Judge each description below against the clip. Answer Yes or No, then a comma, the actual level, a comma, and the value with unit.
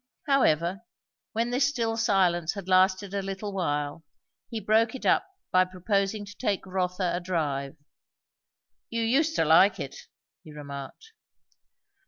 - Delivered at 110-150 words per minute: Yes, average, 140 wpm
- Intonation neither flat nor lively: Yes, average, 4.6 semitones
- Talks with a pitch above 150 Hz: Yes, high, 190 Hz